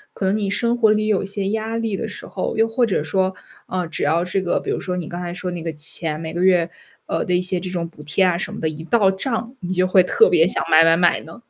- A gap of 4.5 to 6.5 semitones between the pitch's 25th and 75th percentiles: No, average, 3.3 semitones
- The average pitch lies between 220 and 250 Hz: No, medium, 185 Hz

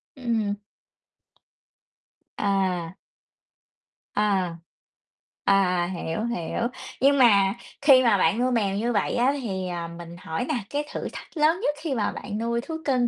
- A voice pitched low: No, high, 210 Hz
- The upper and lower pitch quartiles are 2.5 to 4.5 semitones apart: No, average, 5.3 semitones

